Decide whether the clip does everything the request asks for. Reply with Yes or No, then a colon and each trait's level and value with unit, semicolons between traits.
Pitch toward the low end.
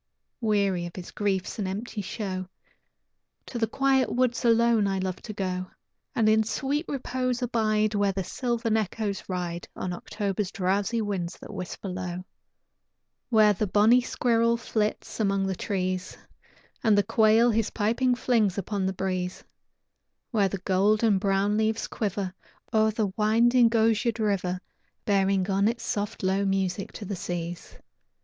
No: high, 205 Hz